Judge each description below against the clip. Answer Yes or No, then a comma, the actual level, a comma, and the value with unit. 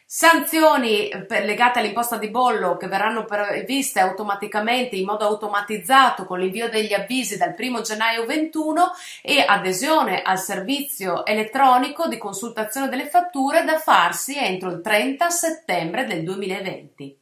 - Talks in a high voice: Yes, high, 220 Hz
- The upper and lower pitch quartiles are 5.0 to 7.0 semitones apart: Yes, average, 5.3 semitones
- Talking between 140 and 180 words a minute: No, average, 130 wpm